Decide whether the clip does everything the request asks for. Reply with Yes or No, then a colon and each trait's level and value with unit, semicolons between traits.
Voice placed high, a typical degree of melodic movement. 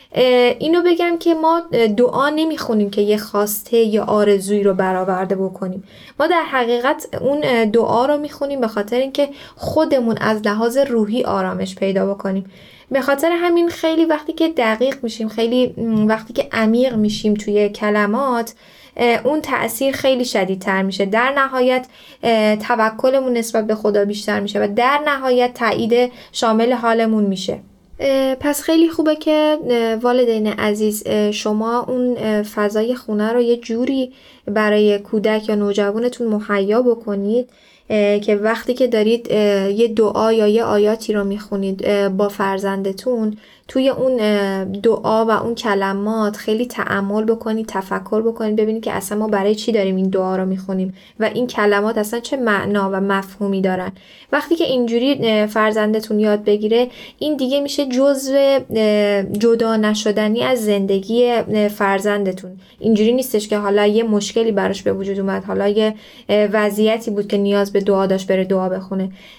Yes: high, 220 Hz; average, 3.2 semitones